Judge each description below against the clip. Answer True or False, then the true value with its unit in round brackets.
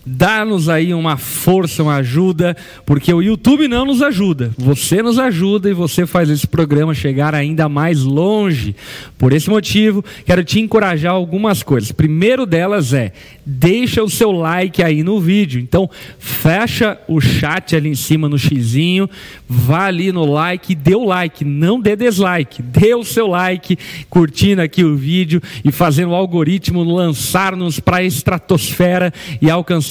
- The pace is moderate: True (160 wpm)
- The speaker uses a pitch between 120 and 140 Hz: False (175 Hz)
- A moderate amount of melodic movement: True (4.2 semitones)